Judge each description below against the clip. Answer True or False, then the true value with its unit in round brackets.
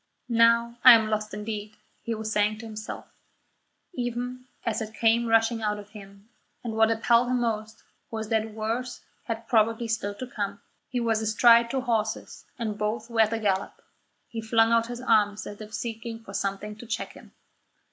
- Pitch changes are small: True (1.5 semitones)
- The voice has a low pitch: False (225 Hz)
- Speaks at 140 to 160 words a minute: False (185 wpm)